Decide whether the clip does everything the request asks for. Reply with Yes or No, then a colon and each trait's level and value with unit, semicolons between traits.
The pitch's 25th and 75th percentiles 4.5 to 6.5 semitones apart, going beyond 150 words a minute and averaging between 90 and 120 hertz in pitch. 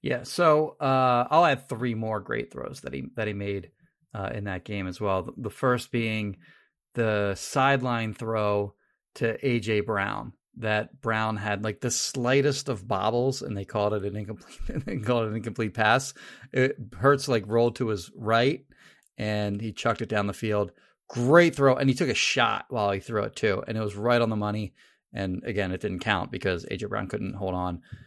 No: average, 3.5 semitones; average, 200 wpm; low, 110 Hz